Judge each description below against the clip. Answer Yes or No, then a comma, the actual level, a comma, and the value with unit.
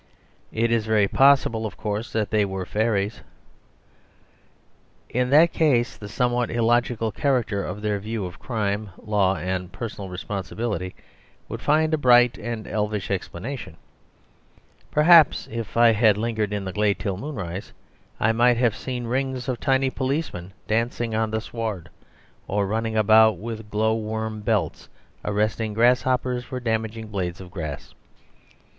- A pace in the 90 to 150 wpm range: Yes, average, 145 wpm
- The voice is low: Yes, low, 110 Hz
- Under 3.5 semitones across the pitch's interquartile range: Yes, average, 2.8 semitones